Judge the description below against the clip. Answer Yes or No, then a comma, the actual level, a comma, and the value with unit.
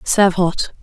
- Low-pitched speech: No, medium, 185 Hz